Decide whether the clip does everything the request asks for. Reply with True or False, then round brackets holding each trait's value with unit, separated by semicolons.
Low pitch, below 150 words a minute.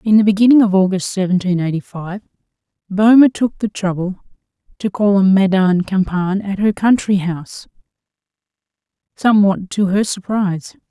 False (195 Hz; 140 wpm)